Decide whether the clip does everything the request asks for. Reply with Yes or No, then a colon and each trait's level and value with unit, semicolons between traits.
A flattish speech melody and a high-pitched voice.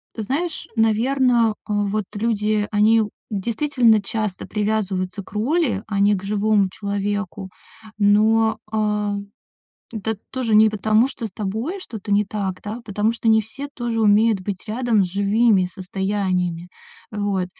Yes: narrow, 1.9 semitones; high, 210 Hz